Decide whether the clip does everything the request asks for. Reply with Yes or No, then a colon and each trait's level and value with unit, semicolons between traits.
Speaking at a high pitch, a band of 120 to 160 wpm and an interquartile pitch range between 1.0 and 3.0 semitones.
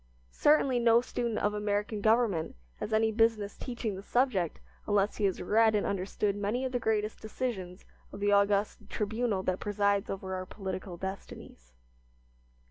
Yes: high, 205 Hz; average, 155 wpm; narrow, 2.5 semitones